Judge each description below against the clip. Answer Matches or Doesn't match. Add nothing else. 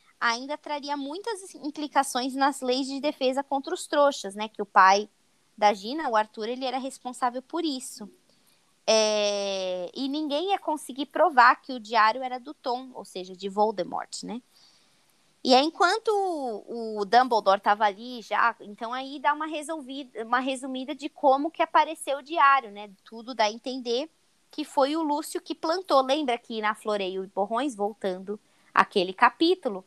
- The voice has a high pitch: Matches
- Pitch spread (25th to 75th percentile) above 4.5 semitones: Matches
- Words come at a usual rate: Matches